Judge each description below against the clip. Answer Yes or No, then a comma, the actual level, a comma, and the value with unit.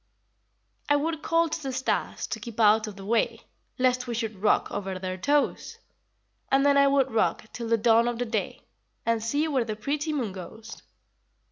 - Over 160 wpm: Yes, average, 195 wpm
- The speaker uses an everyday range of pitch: Yes, average, 4.4 semitones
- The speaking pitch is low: No, high, 235 Hz